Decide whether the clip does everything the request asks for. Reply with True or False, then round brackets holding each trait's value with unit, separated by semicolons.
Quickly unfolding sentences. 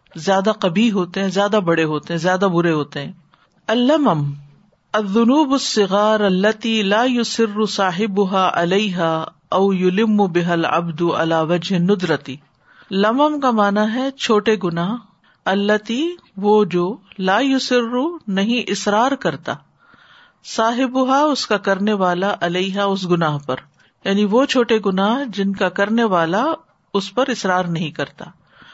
False (135 wpm)